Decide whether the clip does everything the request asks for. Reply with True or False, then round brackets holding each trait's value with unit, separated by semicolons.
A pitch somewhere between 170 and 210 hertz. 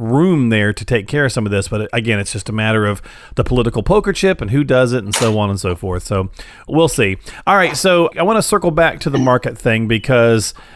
False (120 Hz)